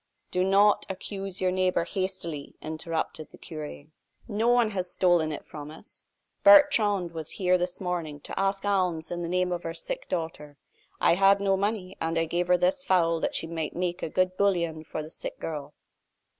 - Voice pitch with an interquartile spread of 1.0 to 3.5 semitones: Yes, average, 3.1 semitones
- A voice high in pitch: No, medium, 180 Hz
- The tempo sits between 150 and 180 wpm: No, average, 190 wpm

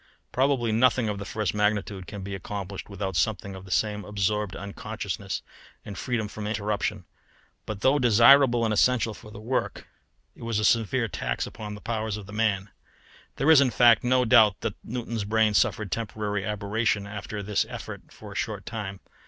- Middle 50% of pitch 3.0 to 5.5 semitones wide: No, narrow, 2.4 semitones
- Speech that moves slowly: No, average, 180 wpm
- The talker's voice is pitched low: Yes, low, 105 Hz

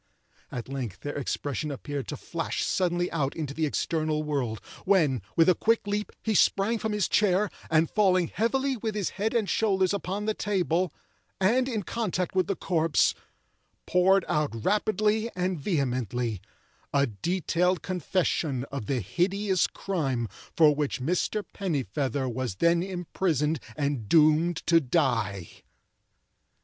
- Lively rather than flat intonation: Yes, wide, 5.7 semitones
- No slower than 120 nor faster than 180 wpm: Yes, average, 140 wpm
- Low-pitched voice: No, medium, 170 Hz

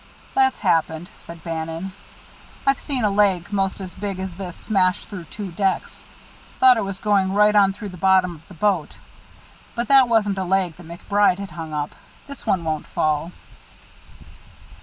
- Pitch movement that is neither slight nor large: Yes, average, 3.4 semitones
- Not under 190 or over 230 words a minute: No, average, 175 wpm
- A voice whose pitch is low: No, high, 190 Hz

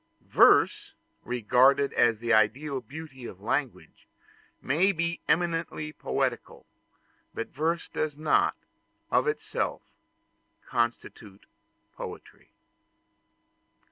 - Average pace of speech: No, slow, 85 wpm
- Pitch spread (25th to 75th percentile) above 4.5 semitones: Yes, wide, 5.4 semitones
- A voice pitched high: No, medium, 140 Hz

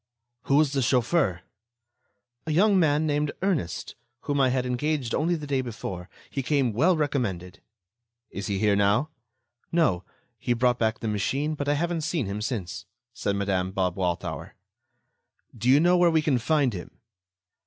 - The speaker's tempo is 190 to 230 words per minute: No, average, 165 wpm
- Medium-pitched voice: No, low, 130 Hz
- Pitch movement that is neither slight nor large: No, wide, 6.9 semitones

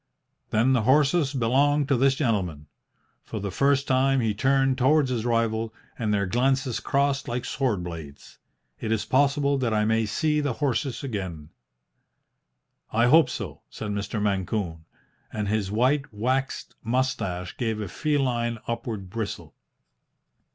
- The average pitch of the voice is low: Yes, low, 120 Hz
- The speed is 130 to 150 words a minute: Yes, average, 145 wpm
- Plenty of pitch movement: No, average, 4.4 semitones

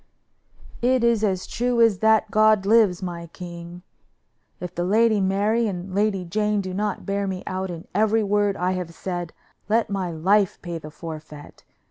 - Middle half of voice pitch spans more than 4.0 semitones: No, average, 3.3 semitones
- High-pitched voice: Yes, high, 195 Hz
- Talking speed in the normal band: Yes, average, 170 wpm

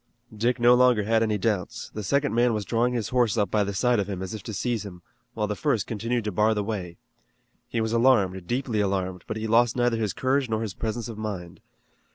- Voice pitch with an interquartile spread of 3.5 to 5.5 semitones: No, average, 2.9 semitones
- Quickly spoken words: Yes, fast, 235 wpm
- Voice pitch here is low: Yes, low, 110 Hz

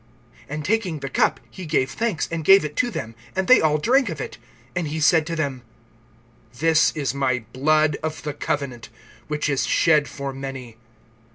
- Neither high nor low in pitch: Yes, medium, 150 Hz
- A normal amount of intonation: Yes, average, 3.1 semitones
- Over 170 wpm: Yes, average, 185 wpm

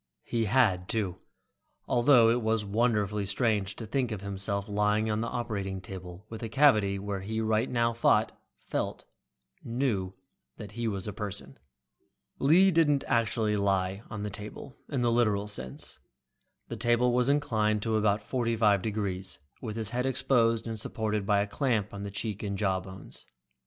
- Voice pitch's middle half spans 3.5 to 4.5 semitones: No, average, 2.8 semitones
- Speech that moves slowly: No, average, 170 wpm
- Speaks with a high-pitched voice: No, low, 110 Hz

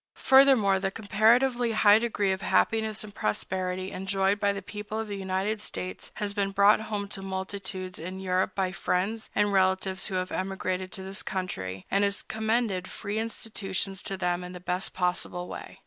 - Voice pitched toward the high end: Yes, high, 195 Hz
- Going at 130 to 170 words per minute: No, average, 180 wpm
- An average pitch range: No, narrow, 2.0 semitones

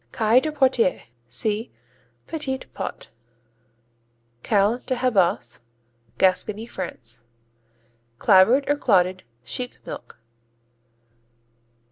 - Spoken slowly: Yes, slow, 80 wpm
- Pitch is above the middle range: Yes, high, 215 Hz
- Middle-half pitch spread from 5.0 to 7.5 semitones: Yes, wide, 5.6 semitones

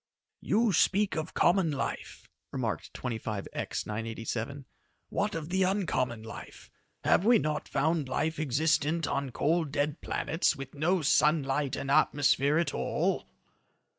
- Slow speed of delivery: Yes, slow, 130 wpm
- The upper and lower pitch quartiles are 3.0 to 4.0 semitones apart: Yes, average, 3.4 semitones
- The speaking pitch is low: No, medium, 150 Hz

